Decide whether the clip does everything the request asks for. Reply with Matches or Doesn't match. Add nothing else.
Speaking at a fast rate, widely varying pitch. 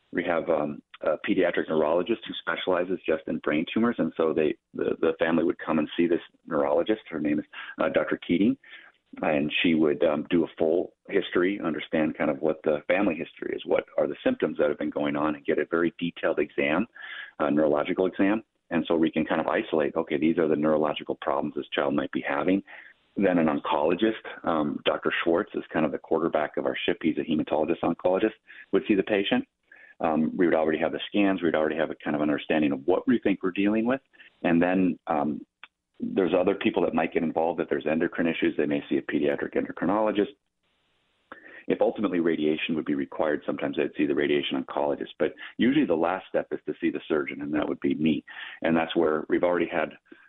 Matches